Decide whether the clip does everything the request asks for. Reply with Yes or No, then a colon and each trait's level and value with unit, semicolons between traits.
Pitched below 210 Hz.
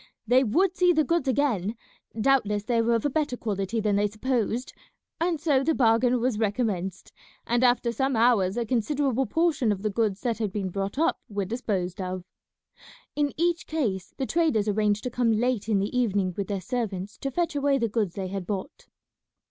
No: high, 230 Hz